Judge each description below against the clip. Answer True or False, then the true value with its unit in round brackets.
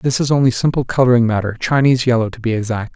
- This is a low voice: True (120 Hz)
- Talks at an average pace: False (225 wpm)